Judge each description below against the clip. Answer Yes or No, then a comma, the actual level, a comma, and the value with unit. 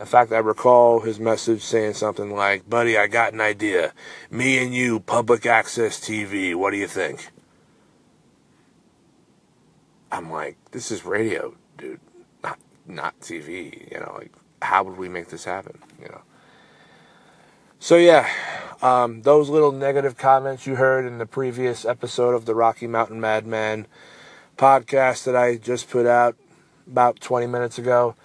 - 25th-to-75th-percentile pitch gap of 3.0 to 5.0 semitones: No, narrow, 2.5 semitones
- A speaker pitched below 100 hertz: No, low, 120 Hz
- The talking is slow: No, average, 155 wpm